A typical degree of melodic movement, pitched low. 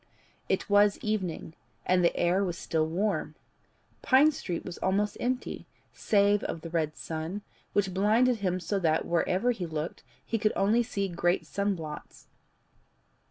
No: average, 3.6 semitones; high, 190 Hz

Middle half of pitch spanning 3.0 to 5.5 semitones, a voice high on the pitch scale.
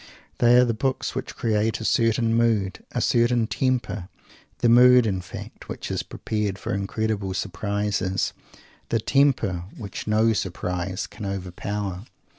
No: average, 3.3 semitones; low, 105 Hz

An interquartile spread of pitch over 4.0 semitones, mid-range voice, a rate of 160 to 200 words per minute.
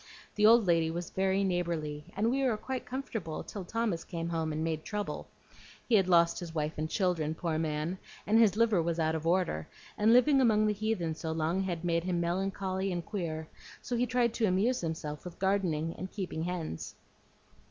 Yes: average, 4.5 semitones; medium, 180 Hz; average, 195 wpm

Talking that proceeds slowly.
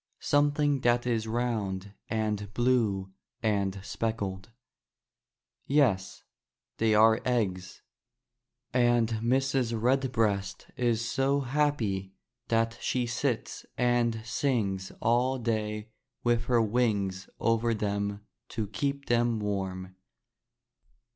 Yes: slow, 95 wpm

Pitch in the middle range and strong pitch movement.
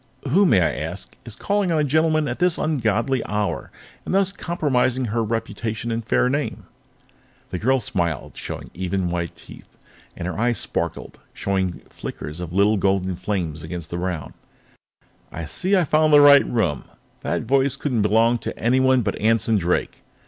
No: low, 115 Hz; wide, 6.8 semitones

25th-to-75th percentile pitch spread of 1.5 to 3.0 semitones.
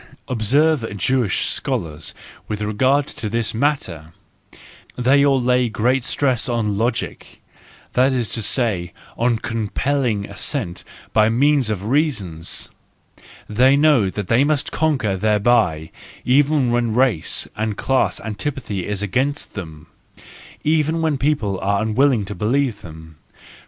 No: average, 4.8 semitones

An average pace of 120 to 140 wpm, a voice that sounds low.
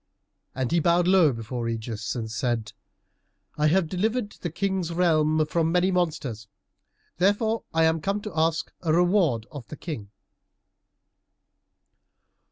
No: slow, 135 wpm; medium, 160 Hz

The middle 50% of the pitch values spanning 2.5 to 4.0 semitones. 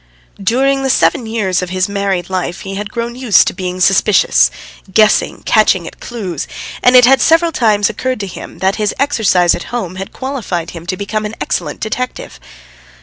No: average, 4.7 semitones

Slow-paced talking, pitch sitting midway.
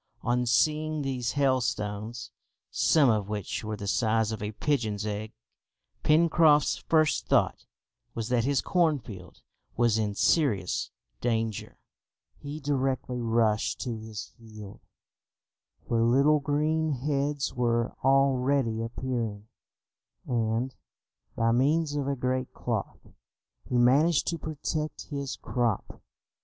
No: slow, 115 wpm; low, 125 Hz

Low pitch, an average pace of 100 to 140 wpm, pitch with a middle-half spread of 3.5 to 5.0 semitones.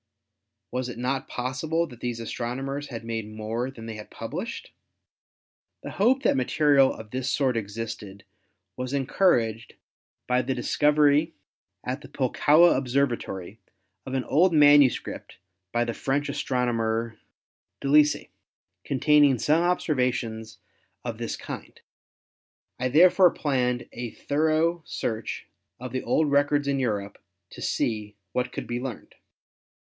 Yes: low, 130 Hz; slow, 135 wpm; average, 3.8 semitones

